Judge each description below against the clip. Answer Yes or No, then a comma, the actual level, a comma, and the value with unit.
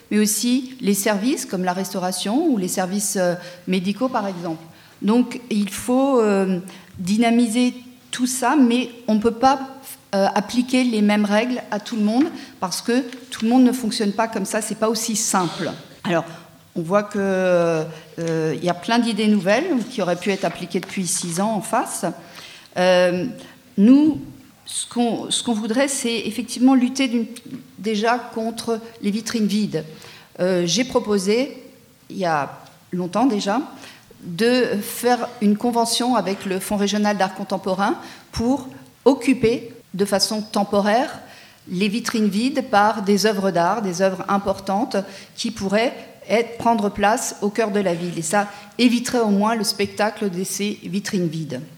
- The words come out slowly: No, average, 155 wpm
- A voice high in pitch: Yes, high, 210 Hz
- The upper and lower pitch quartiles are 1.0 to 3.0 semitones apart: No, average, 3.7 semitones